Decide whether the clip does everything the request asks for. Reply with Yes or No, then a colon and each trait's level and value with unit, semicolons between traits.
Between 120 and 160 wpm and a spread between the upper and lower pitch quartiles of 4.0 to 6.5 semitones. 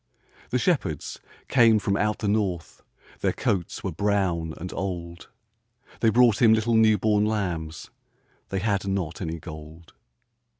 Yes: average, 140 wpm; average, 4.3 semitones